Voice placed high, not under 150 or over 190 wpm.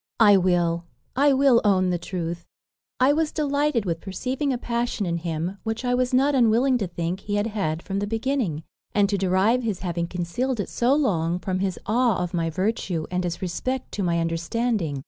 No: high, 200 Hz; average, 200 wpm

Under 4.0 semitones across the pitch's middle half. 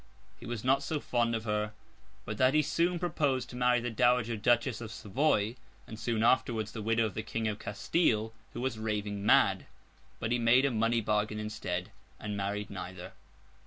Yes: average, 2.7 semitones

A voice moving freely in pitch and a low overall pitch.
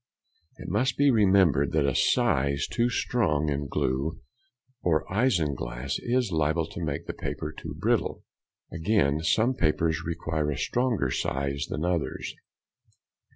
Yes: wide, 6.1 semitones; very low, 80 Hz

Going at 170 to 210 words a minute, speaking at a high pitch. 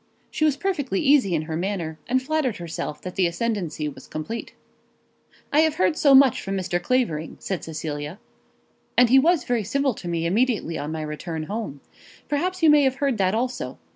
Yes: average, 190 wpm; high, 205 Hz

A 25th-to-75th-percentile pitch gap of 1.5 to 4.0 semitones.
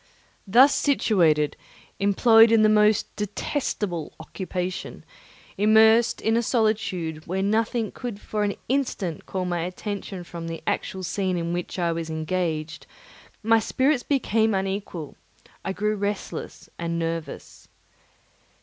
No: average, 4.5 semitones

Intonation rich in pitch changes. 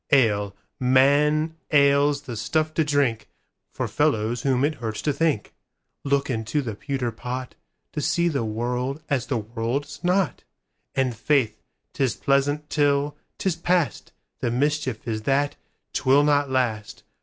No: average, 3.7 semitones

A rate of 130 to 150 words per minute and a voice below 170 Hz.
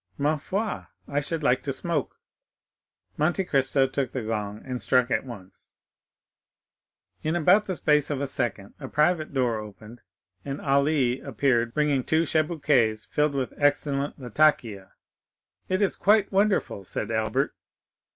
Yes: average, 140 wpm; medium, 140 Hz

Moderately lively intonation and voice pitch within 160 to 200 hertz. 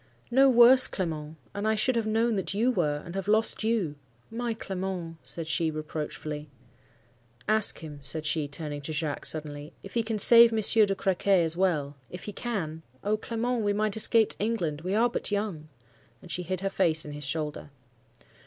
No: wide, 5.9 semitones; medium, 185 Hz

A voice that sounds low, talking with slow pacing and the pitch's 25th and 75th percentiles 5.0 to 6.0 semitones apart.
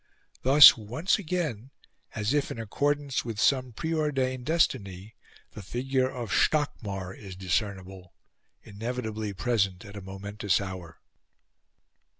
Yes: low, 110 Hz; slow, 115 wpm; average, 5.3 semitones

